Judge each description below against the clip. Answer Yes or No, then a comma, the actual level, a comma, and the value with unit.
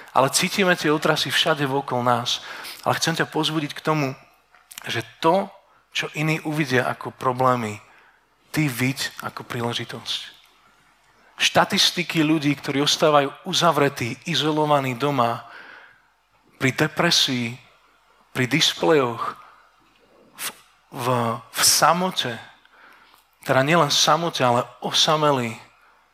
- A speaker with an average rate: No, slow, 105 wpm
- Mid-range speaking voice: Yes, medium, 145 Hz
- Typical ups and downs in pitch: Yes, average, 3.9 semitones